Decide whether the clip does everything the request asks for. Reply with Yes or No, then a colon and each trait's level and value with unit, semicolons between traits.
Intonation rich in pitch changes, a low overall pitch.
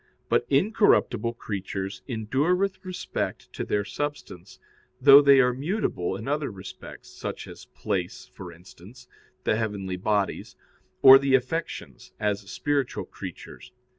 Yes: wide, 6.3 semitones; low, 120 Hz